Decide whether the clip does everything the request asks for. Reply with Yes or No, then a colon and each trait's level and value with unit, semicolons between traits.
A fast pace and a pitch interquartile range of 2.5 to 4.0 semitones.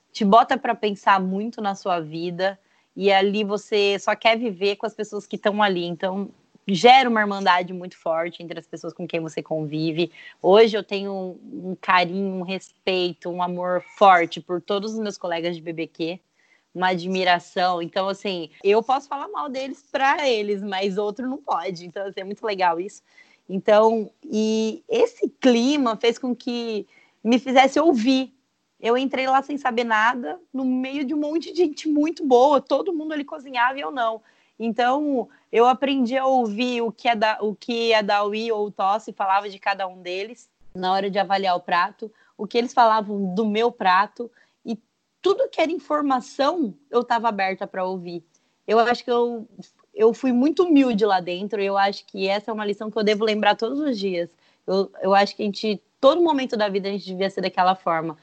No: fast, 195 wpm; average, 4.5 semitones